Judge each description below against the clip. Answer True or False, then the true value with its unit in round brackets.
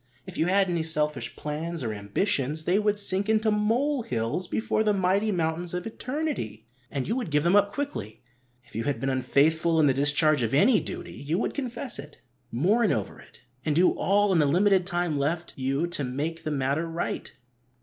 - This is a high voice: False (165 Hz)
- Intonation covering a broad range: True (6.2 semitones)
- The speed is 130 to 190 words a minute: False (200 wpm)